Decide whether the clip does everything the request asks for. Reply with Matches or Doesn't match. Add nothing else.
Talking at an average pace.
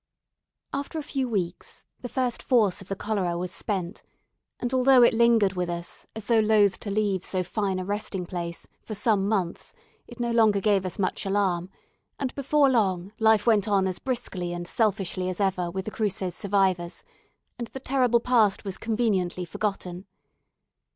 Matches